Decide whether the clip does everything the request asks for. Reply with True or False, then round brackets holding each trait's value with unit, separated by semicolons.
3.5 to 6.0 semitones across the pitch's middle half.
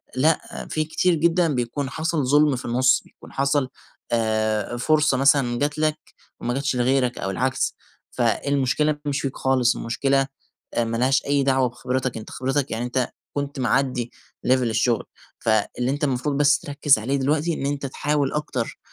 False (2.9 semitones)